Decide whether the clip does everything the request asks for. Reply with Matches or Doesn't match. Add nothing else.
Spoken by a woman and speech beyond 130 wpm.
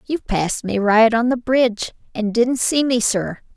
Matches